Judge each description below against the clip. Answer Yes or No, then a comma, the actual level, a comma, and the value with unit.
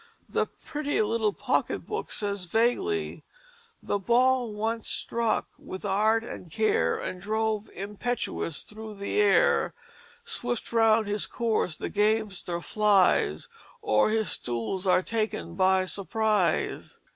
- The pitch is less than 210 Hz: No, high, 215 Hz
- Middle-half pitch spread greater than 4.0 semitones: No, narrow, 2.6 semitones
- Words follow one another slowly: Yes, slow, 120 wpm